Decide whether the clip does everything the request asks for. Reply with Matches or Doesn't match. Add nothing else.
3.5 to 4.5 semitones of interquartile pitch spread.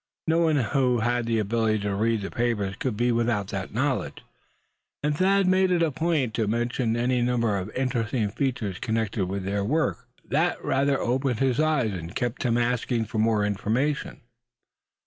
Matches